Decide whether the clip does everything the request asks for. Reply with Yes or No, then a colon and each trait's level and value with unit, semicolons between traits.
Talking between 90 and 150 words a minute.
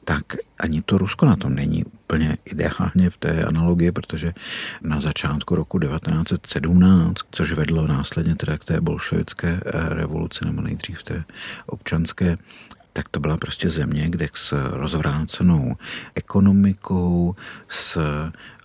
Yes: average, 125 wpm